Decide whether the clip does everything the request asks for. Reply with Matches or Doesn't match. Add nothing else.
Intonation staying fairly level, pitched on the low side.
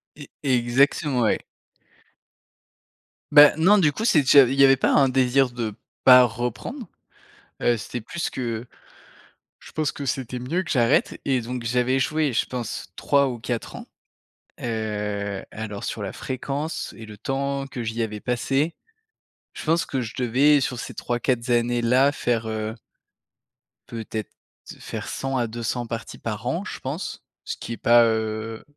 Doesn't match